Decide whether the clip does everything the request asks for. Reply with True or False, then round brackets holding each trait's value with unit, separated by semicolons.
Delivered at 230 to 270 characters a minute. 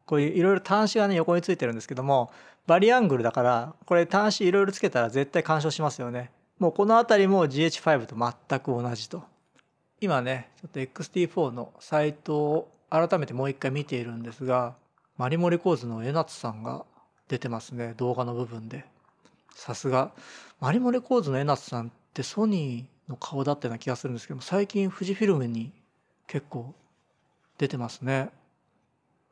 False (350 characters per minute)